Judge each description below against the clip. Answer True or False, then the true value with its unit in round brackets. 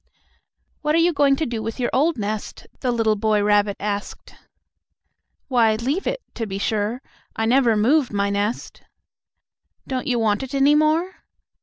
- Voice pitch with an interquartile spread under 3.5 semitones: False (4.8 semitones)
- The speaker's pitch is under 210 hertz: False (235 Hz)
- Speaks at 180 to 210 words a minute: False (165 wpm)